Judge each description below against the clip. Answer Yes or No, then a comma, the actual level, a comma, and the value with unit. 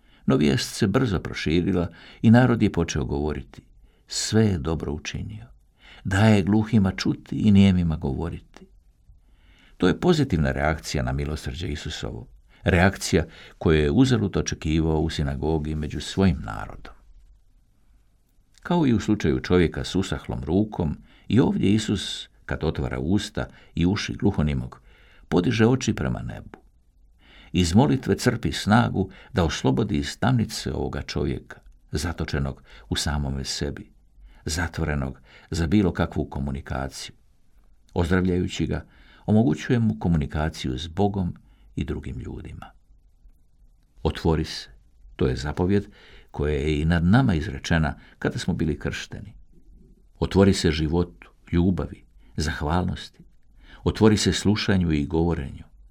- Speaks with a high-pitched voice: No, very low, 85 Hz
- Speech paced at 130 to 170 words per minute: No, average, 120 wpm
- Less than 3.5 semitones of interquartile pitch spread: No, average, 4.8 semitones